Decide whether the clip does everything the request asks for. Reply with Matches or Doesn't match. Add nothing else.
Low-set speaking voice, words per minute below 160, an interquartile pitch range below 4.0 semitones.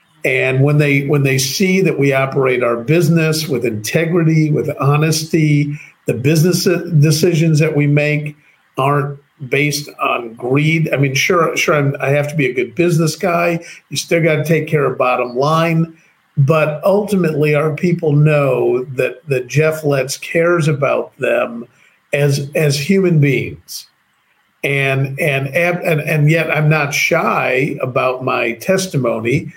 Doesn't match